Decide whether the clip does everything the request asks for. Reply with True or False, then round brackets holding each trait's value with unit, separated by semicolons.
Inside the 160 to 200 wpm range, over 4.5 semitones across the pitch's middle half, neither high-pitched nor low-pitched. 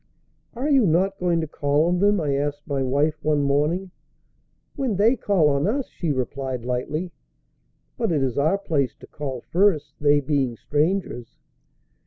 True (165 wpm; 4.9 semitones; 150 Hz)